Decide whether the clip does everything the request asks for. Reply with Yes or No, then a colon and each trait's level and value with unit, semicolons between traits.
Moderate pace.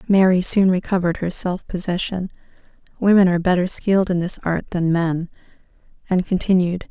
No: slow, 130 wpm